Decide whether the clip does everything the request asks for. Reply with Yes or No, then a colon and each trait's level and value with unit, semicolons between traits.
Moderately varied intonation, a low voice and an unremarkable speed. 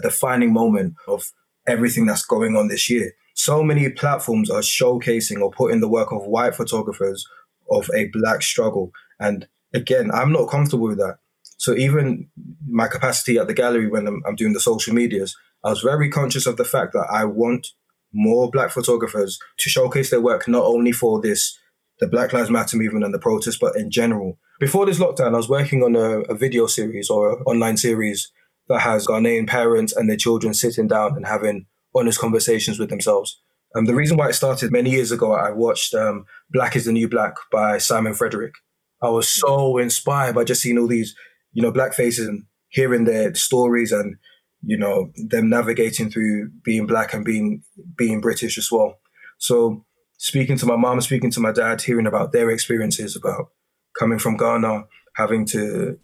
Yes: average, 3.8 semitones; low, 120 Hz; average, 190 wpm